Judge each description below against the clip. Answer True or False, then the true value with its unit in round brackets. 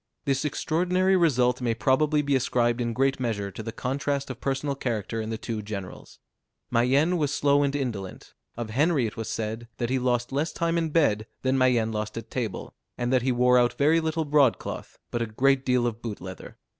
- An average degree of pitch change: True (3.7 semitones)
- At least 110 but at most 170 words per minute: False (205 wpm)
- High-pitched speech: False (125 Hz)